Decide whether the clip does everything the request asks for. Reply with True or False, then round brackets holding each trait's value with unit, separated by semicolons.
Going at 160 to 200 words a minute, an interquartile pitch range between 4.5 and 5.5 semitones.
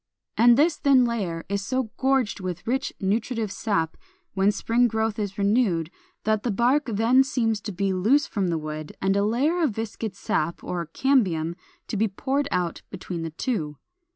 True (180 wpm; 5.0 semitones)